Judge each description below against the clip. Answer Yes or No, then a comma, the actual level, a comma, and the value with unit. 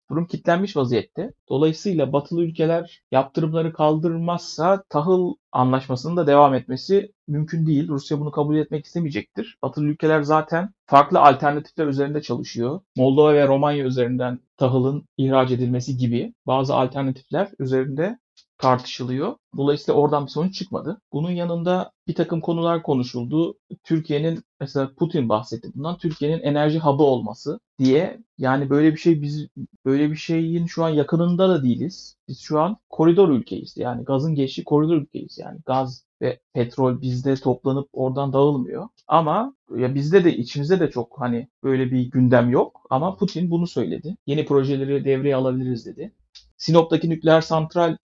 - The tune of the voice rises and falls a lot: No, average, 4.0 semitones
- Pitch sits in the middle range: Yes, medium, 150 Hz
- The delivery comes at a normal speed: No, fast, 145 wpm